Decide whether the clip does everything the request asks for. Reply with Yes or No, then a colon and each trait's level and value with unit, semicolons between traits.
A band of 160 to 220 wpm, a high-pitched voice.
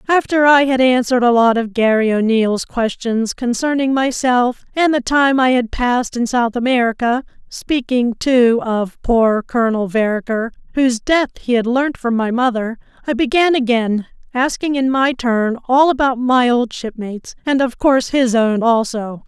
Yes: average, 165 wpm; high, 245 Hz